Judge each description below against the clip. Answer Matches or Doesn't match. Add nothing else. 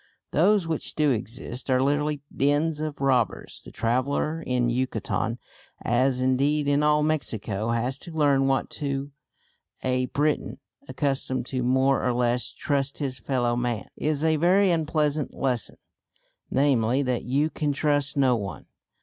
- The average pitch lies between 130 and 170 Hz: Matches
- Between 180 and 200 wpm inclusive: Doesn't match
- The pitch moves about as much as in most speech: Matches